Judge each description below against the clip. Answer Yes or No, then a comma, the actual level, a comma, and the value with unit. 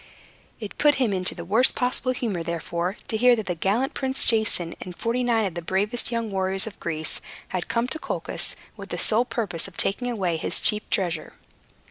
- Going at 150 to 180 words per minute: No, average, 200 wpm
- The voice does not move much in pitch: No, average, 5.1 semitones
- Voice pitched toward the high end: Yes, high, 210 Hz